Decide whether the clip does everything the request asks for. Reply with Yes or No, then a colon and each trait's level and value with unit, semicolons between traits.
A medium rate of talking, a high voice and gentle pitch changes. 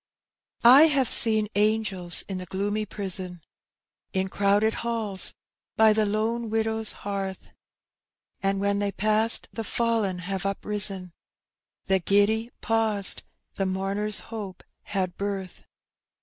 No: slow, 120 wpm; high, 205 Hz; narrow, 2.3 semitones